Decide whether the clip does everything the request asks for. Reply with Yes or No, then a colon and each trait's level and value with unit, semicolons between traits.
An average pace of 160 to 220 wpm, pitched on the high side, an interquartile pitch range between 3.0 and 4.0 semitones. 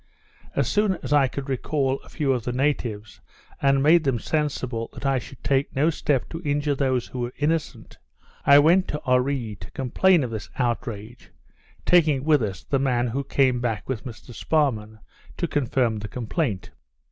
No: average, 180 wpm; low, 135 Hz; average, 3.5 semitones